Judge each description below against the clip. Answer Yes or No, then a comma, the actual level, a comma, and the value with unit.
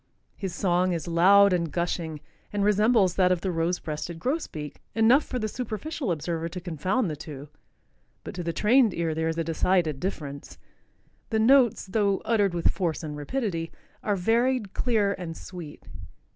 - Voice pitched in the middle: Yes, medium, 180 Hz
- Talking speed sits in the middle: Yes, average, 170 wpm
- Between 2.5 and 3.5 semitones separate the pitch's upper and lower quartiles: No, average, 4.7 semitones